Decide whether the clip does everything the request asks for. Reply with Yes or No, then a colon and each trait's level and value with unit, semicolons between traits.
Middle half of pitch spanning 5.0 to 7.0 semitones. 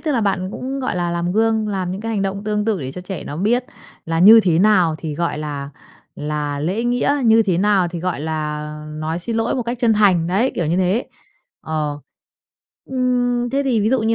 Yes: wide, 5.5 semitones